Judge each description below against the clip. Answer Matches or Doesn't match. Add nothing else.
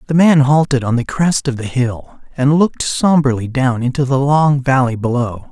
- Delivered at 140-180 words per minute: Doesn't match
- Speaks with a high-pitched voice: Doesn't match